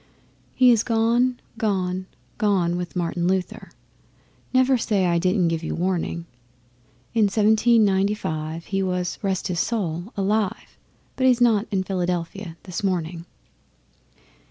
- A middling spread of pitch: Yes, average, 3.8 semitones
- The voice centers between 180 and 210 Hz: Yes, high, 190 Hz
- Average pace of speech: No, slow, 130 wpm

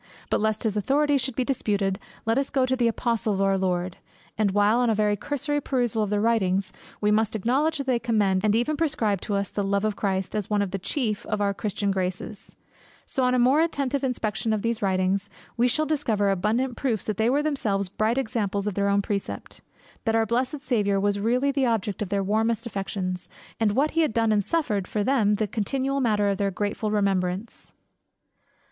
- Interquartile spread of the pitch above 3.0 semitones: Yes, average, 4.0 semitones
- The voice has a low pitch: No, high, 215 Hz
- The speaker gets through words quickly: Yes, fast, 215 wpm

